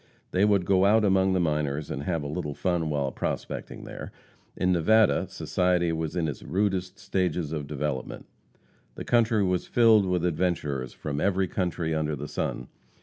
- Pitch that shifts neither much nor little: Yes, average, 4.0 semitones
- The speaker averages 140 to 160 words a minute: No, average, 170 wpm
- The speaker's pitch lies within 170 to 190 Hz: No, very low, 90 Hz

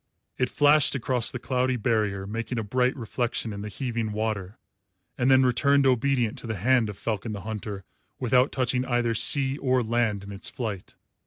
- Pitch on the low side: Yes, low, 120 Hz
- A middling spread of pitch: Yes, average, 3.2 semitones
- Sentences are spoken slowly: No, average, 180 wpm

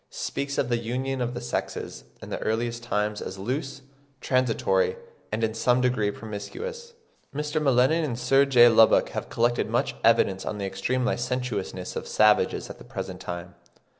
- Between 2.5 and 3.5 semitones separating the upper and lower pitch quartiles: No, average, 3.9 semitones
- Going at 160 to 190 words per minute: Yes, average, 170 wpm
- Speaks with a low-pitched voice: Yes, low, 120 Hz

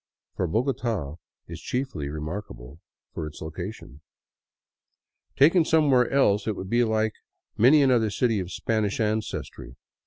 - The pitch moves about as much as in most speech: No, wide, 6.9 semitones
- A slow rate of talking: Yes, slow, 125 wpm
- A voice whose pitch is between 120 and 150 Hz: No, low, 110 Hz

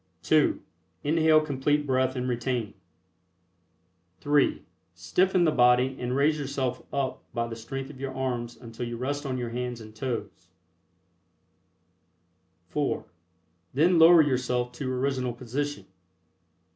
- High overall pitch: No, low, 130 Hz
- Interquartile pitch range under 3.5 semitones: Yes, average, 2.9 semitones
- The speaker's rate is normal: No, slow, 125 wpm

